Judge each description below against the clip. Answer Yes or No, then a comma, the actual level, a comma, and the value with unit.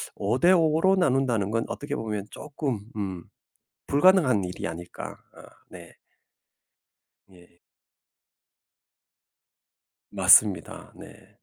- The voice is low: Yes, low, 110 Hz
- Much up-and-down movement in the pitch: Yes, wide, 7.7 semitones